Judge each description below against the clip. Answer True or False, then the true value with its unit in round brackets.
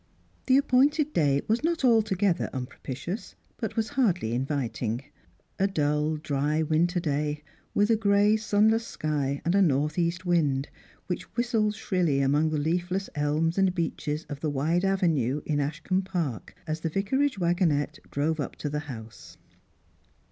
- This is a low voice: False (165 Hz)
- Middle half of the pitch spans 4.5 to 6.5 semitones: True (5.2 semitones)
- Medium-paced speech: True (155 wpm)